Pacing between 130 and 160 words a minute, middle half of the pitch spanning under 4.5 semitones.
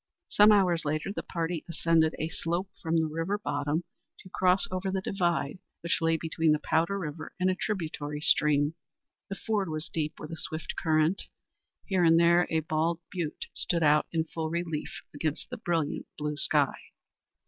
No: average, 175 wpm; narrow, 2.6 semitones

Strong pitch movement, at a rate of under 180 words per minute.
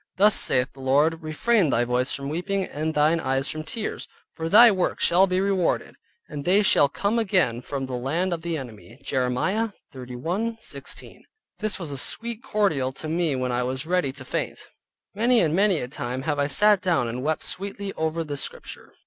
No: wide, 6.5 semitones; average, 190 wpm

